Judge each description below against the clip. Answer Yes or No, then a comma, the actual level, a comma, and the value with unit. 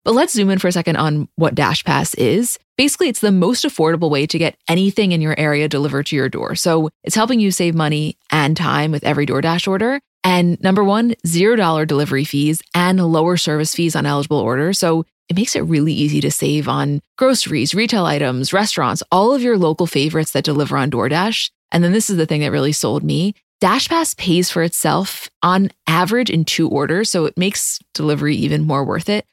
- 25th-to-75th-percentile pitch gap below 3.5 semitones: No, average, 4.5 semitones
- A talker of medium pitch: Yes, medium, 165 Hz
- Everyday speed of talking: No, fast, 215 wpm